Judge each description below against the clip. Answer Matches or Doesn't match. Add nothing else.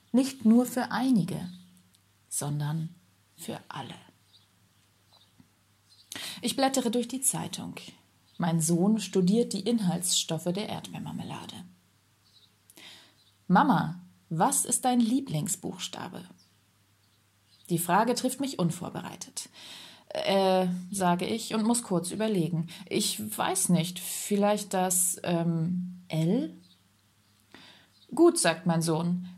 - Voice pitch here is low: Doesn't match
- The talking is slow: Matches